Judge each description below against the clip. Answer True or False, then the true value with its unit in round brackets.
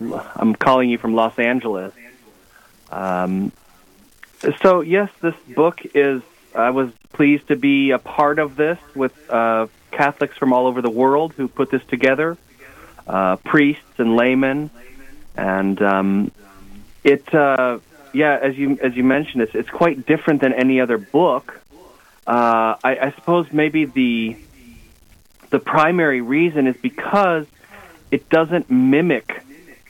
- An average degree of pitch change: True (4.5 semitones)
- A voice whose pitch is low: True (130 Hz)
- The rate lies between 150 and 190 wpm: False (140 wpm)